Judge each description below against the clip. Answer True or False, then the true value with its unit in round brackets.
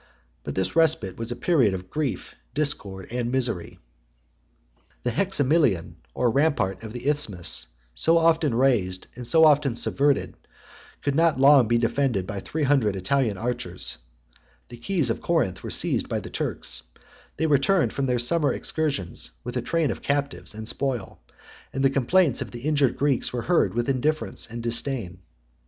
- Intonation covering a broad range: False (4.6 semitones)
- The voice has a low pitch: True (130 Hz)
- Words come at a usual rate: True (165 wpm)